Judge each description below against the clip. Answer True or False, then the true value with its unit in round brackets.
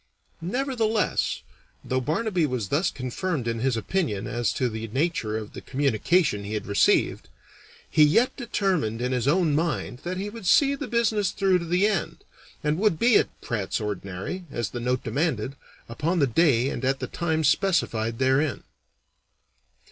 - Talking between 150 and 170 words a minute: True (165 wpm)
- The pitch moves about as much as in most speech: False (7.8 semitones)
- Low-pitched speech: False (150 Hz)